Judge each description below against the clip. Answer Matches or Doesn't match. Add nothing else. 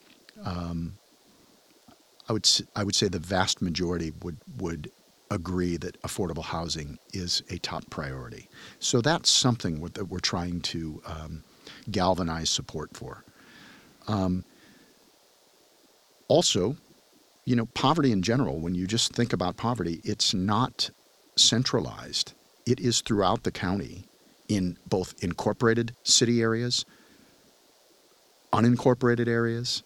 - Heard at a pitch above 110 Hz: Doesn't match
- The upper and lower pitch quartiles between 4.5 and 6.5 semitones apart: Matches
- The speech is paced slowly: Matches